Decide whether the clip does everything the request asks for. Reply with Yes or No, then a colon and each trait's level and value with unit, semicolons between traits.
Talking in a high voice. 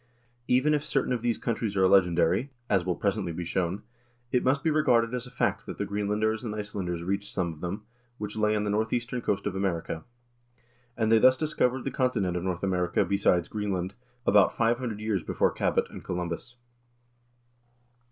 No: low, 105 Hz